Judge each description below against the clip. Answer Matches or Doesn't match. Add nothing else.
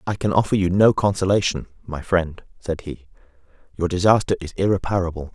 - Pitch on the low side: Matches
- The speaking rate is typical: Matches